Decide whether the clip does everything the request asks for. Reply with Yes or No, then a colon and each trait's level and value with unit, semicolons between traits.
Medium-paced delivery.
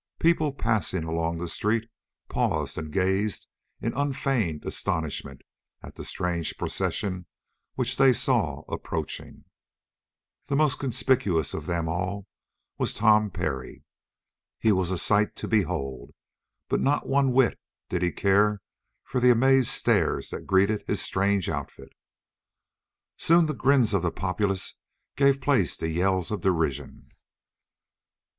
No: slow, 130 wpm